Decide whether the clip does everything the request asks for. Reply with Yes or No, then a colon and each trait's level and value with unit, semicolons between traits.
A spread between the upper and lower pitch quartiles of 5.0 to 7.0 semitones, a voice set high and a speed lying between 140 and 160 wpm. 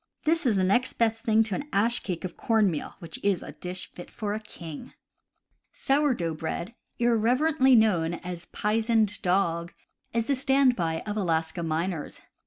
No: wide, 5.4 semitones; high, 210 Hz; average, 180 wpm